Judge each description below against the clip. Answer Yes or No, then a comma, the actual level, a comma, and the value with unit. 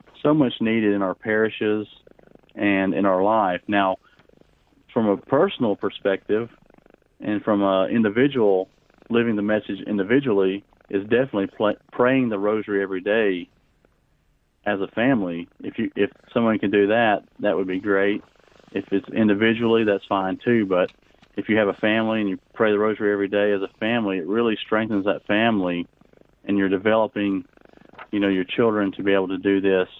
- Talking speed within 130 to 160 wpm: No, average, 170 wpm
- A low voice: Yes, low, 100 Hz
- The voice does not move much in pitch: Yes, narrow, 2.2 semitones